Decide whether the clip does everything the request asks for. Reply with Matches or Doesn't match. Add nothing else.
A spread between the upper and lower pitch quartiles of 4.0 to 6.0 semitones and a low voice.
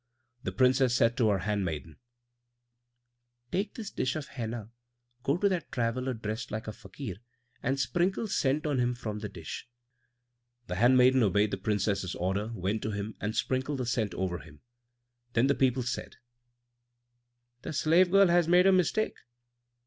Matches